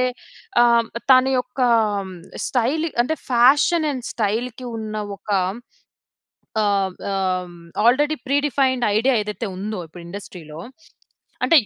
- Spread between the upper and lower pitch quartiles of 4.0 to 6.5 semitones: Yes, average, 4.5 semitones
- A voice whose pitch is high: Yes, high, 235 Hz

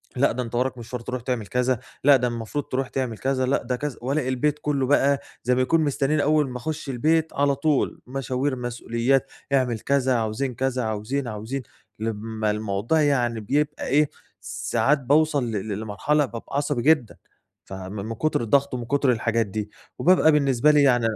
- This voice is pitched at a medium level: No, low, 130 Hz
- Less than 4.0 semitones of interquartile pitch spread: Yes, average, 3.6 semitones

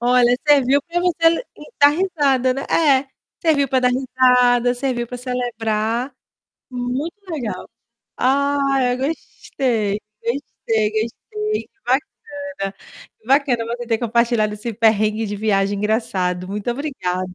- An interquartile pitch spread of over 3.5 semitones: Yes, average, 4.1 semitones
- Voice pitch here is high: Yes, high, 245 Hz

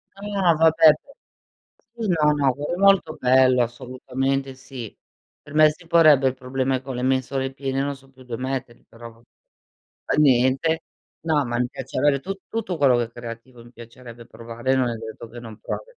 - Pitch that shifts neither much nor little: Yes, average, 3.7 semitones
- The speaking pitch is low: Yes, low, 130 Hz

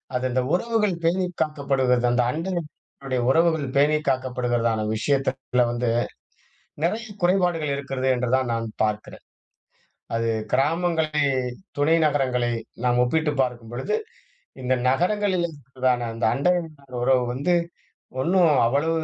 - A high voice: No, low, 135 Hz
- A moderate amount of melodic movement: Yes, average, 4.6 semitones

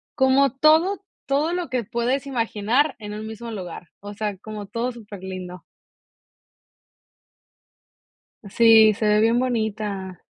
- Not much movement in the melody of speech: No, average, 3.8 semitones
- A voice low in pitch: No, high, 225 Hz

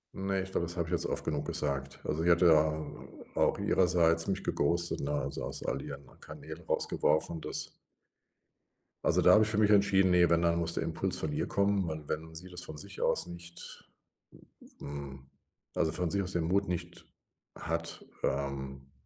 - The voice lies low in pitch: Yes, very low, 85 Hz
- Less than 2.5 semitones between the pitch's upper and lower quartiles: No, average, 2.8 semitones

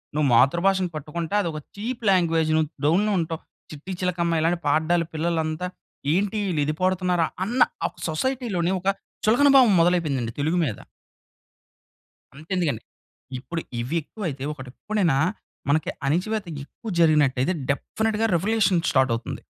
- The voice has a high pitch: No, medium, 170 Hz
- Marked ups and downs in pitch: No, average, 4.0 semitones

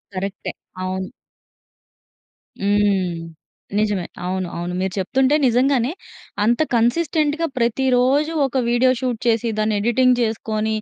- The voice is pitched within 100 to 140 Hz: No, high, 230 Hz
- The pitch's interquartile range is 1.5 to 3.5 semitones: No, average, 4.5 semitones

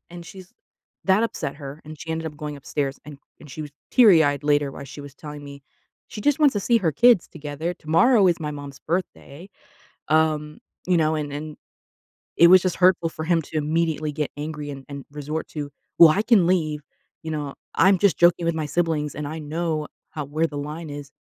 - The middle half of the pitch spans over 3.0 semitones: No, average, 2.7 semitones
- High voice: No, medium, 155 Hz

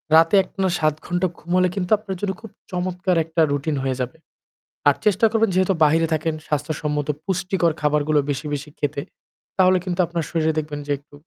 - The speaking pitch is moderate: Yes, medium, 165 Hz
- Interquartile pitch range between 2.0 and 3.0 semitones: No, average, 3.8 semitones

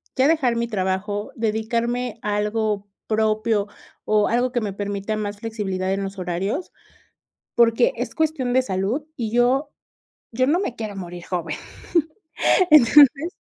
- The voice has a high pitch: Yes, high, 220 Hz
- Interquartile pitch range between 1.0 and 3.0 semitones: No, average, 3.5 semitones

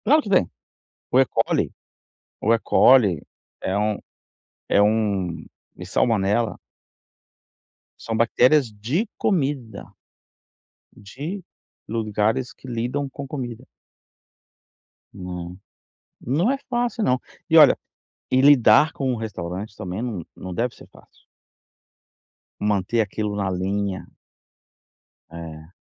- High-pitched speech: No, low, 110 Hz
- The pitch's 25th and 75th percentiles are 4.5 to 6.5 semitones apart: Yes, average, 4.9 semitones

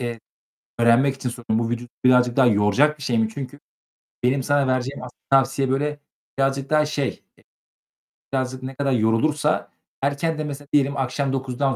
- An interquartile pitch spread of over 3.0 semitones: No, narrow, 2.5 semitones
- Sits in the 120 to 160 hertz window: Yes, low, 135 Hz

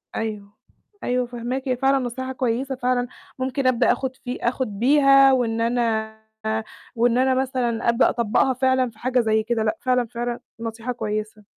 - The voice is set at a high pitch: Yes, high, 245 Hz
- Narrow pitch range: Yes, narrow, 2.3 semitones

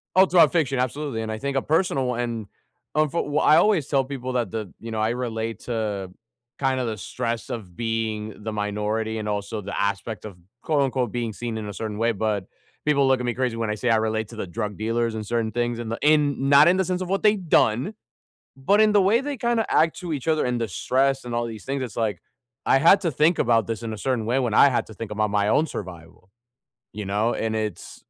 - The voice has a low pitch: Yes, low, 120 Hz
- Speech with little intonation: No, average, 4.3 semitones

